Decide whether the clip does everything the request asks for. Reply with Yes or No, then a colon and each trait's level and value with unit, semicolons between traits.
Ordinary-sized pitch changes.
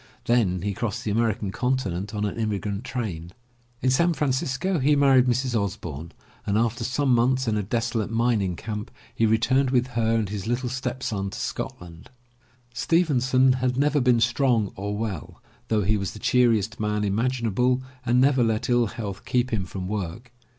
Yes: average, 3.7 semitones